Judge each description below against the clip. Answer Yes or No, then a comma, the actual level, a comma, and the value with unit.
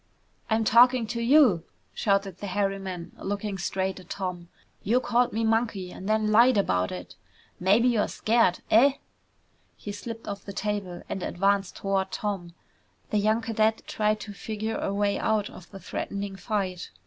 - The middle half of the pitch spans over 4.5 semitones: No, narrow, 2.6 semitones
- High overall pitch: Yes, high, 205 Hz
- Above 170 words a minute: No, average, 165 wpm